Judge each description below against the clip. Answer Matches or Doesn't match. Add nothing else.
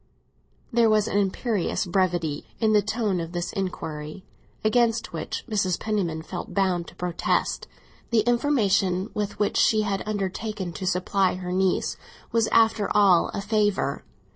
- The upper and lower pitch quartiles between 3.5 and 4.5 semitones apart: Doesn't match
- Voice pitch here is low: Doesn't match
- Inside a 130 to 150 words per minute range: Matches